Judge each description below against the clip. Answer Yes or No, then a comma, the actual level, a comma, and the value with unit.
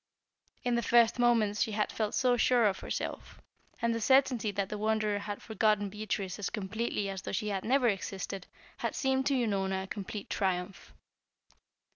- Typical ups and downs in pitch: Yes, average, 3.1 semitones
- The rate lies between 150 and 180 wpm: Yes, average, 170 wpm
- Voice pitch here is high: Yes, high, 210 Hz